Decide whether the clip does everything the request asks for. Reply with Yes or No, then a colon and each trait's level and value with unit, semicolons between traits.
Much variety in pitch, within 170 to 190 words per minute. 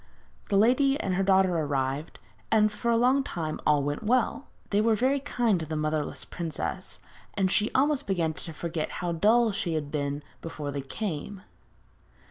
Yes: wide, 6.5 semitones; average, 175 wpm